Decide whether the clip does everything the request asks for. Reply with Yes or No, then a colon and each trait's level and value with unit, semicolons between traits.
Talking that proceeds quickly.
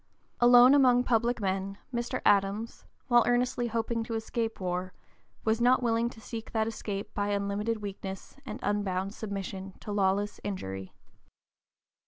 No: average, 140 wpm